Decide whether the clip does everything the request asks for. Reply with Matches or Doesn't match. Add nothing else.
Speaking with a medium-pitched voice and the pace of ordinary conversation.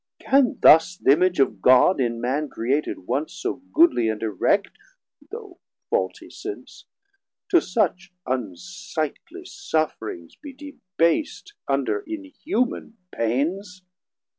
Doesn't match